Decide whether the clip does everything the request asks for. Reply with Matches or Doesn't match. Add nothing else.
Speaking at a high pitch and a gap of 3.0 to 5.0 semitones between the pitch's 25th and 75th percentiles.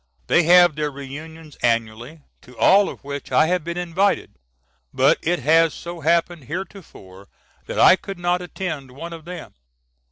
Doesn't match